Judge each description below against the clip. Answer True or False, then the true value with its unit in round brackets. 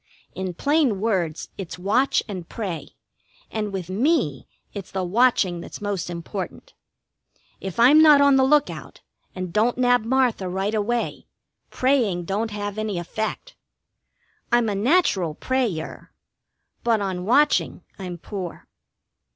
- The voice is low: False (210 Hz)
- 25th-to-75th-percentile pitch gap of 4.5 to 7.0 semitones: True (5.1 semitones)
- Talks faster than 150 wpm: False (135 wpm)